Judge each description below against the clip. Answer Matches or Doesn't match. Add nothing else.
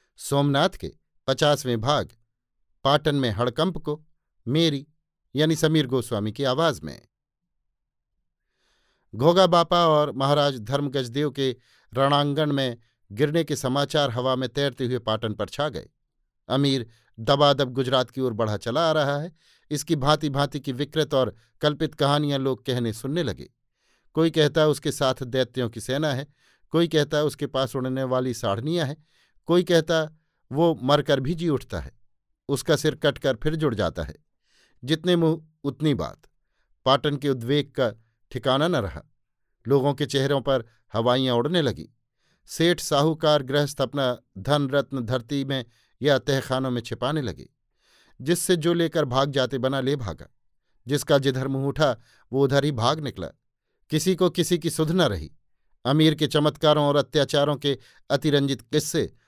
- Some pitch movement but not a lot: Matches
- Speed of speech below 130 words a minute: Doesn't match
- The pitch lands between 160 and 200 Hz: Doesn't match